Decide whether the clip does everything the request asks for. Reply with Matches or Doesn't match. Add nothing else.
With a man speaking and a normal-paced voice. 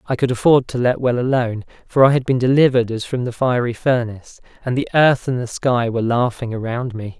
Doesn't match